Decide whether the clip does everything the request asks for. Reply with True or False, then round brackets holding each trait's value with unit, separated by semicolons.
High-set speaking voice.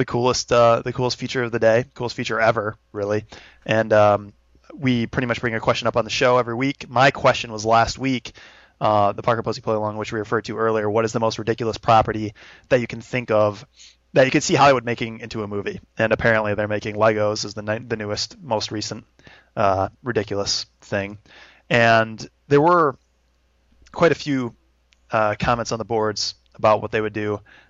False (110 Hz)